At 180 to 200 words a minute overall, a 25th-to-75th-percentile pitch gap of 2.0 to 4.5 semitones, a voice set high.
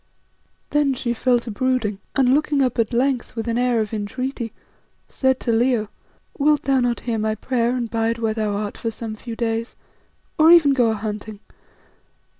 Yes: average, 185 wpm; average, 2.7 semitones; high, 235 Hz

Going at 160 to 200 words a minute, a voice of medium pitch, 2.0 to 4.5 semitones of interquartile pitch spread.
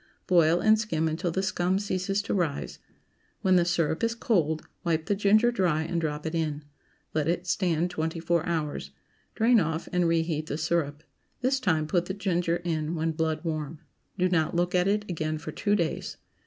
Yes: average, 190 wpm; medium, 170 Hz; average, 2.8 semitones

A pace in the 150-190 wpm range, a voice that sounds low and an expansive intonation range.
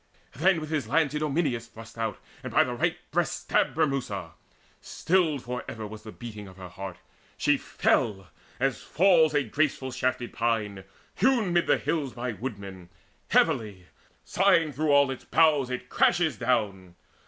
Yes: average, 160 wpm; low, 125 Hz; wide, 6.4 semitones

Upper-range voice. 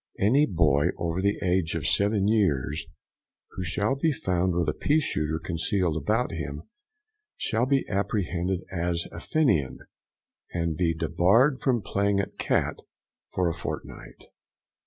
No: very low, 90 Hz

